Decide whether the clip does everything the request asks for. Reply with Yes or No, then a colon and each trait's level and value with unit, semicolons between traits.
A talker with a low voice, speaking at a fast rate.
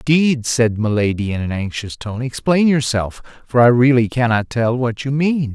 No: low, 125 Hz; average, 185 wpm